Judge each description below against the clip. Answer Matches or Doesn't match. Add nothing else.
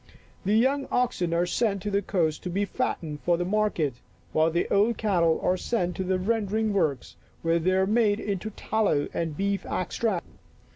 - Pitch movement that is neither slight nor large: Matches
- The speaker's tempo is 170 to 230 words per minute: Matches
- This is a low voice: Doesn't match